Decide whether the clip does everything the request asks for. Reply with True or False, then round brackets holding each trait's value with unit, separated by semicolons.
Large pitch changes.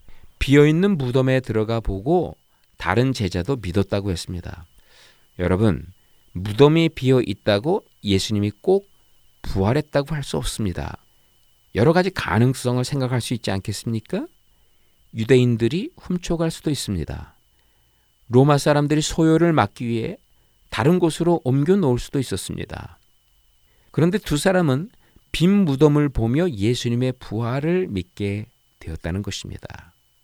True (7.3 semitones)